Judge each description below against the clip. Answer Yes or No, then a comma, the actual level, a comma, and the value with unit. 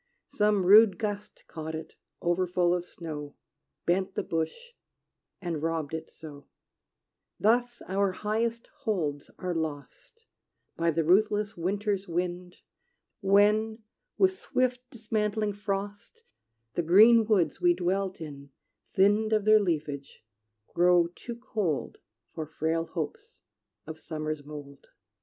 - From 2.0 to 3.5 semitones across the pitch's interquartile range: No, average, 4.7 semitones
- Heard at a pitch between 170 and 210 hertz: Yes, medium, 185 Hz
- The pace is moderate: No, slow, 120 wpm